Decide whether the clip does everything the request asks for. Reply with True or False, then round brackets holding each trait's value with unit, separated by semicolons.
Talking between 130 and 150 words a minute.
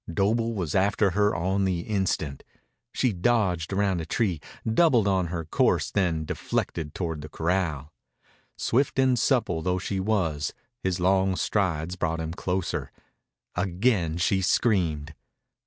True (140 wpm)